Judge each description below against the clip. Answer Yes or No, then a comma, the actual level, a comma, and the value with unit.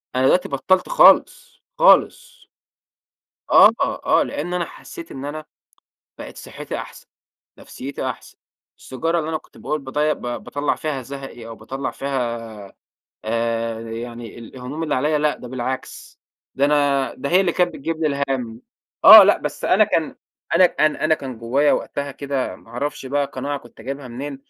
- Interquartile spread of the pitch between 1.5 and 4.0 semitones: Yes, average, 3.6 semitones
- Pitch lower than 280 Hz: Yes, medium, 140 Hz